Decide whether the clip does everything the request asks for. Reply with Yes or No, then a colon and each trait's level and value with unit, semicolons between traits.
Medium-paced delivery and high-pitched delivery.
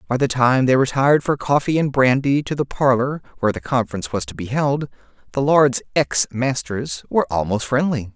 No: average, 190 wpm; low, 130 Hz